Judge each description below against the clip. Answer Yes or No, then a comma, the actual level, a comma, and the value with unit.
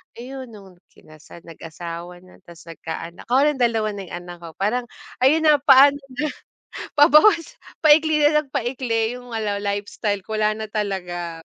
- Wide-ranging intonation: Yes, wide, 7.2 semitones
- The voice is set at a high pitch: Yes, high, 220 Hz